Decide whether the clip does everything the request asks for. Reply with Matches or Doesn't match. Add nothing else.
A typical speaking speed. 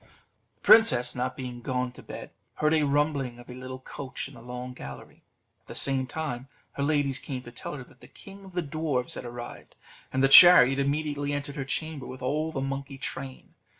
Doesn't match